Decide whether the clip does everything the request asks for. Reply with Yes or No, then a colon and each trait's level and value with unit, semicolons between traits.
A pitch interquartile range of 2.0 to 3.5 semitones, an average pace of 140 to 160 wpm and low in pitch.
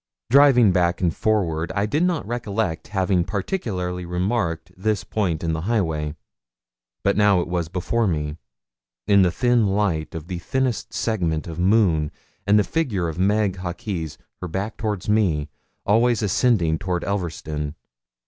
No: average, 4.2 semitones; average, 150 wpm; very low, 95 Hz